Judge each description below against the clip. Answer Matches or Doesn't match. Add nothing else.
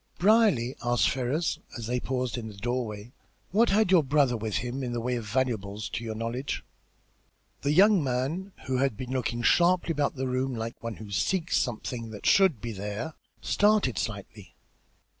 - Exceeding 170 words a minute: Matches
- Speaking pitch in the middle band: Doesn't match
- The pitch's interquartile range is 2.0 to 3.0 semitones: Doesn't match